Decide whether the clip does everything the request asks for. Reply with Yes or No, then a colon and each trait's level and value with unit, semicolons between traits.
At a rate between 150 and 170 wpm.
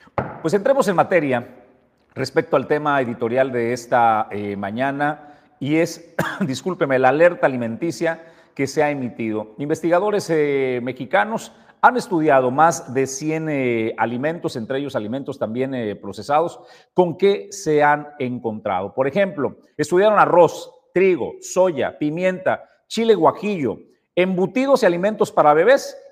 No: average, 130 wpm